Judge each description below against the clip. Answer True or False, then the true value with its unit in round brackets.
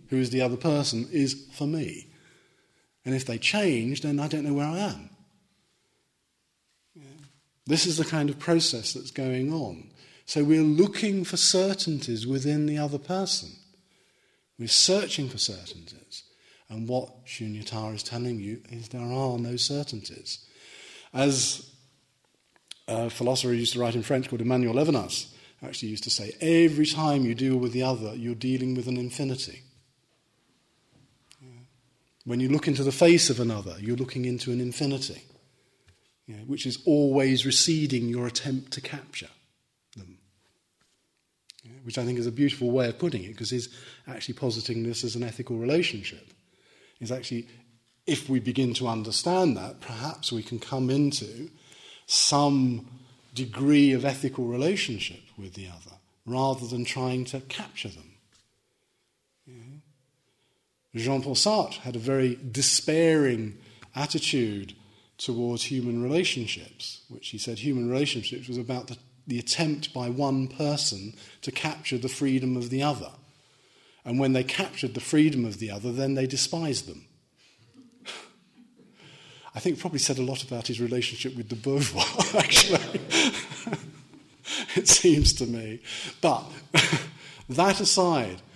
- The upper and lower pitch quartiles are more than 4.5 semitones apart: False (3.3 semitones)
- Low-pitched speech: True (130 Hz)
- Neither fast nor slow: True (145 wpm)